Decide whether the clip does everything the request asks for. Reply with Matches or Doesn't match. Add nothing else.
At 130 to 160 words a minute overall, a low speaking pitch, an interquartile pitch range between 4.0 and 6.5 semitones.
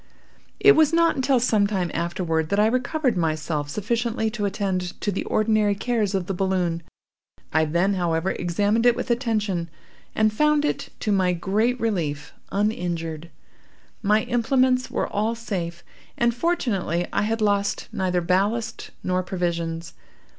Doesn't match